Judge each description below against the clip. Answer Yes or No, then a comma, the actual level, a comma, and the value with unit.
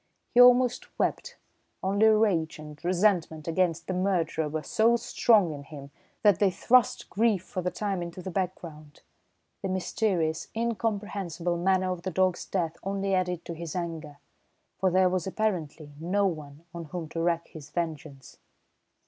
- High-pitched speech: No, medium, 180 Hz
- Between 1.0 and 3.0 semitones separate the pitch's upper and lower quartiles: No, average, 3.5 semitones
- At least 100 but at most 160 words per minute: Yes, average, 155 wpm